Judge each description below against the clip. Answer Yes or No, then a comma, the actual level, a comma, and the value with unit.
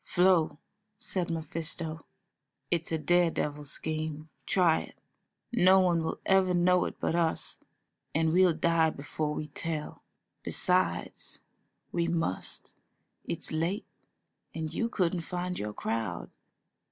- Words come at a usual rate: No, slow, 125 wpm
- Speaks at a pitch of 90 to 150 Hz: No, medium, 165 Hz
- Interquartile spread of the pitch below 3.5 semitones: Yes, narrow, 2.4 semitones